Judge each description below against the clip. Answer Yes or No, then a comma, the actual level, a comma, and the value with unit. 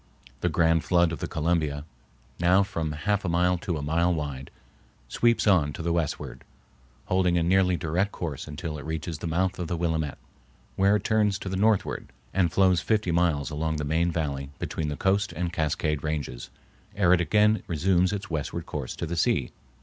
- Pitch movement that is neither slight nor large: Yes, average, 3.2 semitones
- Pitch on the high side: No, very low, 85 Hz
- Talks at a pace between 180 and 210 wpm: Yes, average, 190 wpm